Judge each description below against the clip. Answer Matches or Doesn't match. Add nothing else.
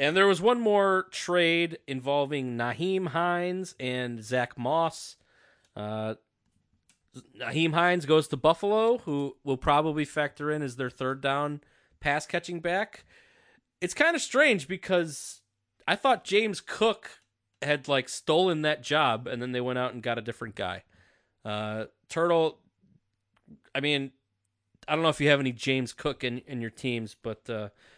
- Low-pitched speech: Doesn't match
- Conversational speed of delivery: Matches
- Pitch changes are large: Matches